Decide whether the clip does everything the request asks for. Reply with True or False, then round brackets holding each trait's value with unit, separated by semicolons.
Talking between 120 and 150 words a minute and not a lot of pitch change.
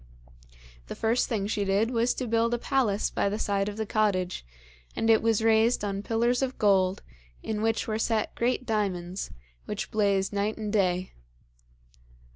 False (170 wpm; 2.2 semitones)